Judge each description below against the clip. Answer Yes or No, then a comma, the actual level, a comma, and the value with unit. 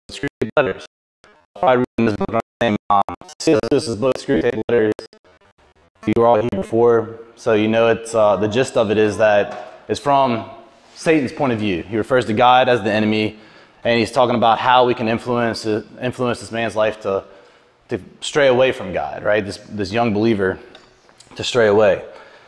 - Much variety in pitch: No, narrow, 2.4 semitones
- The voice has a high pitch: No, low, 115 Hz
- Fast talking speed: No, average, 175 wpm